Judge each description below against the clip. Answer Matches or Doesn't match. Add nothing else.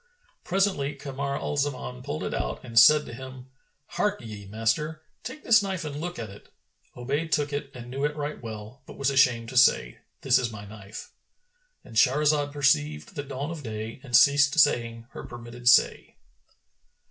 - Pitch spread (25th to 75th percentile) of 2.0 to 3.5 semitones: Doesn't match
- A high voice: Doesn't match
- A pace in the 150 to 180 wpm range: Matches